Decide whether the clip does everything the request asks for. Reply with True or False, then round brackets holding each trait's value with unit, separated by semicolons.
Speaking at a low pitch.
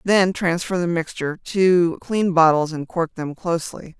False (170 Hz)